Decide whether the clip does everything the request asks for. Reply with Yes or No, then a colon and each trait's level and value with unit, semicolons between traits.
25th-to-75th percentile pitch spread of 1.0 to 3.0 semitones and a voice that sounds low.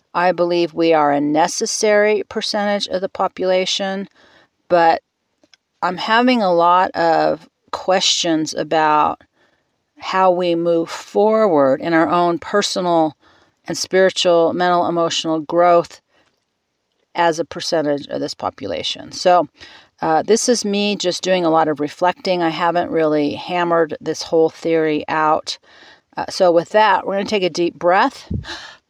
No: narrow, 2.6 semitones; medium, 175 Hz